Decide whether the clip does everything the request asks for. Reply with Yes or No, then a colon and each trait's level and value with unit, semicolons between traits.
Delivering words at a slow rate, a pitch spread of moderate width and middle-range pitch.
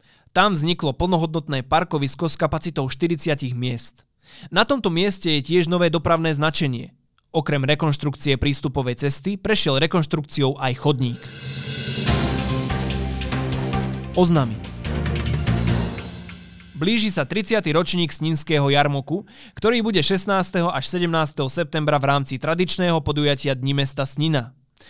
Yes: slow, 105 wpm; average, 4.6 semitones; medium, 150 Hz